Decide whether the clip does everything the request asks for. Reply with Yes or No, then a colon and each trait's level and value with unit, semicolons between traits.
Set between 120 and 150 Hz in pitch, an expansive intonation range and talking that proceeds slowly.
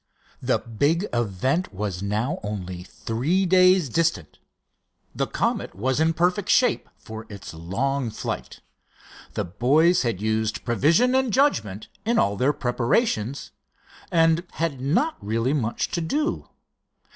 Yes: low, 135 Hz; wide, 8.0 semitones; slow, 130 wpm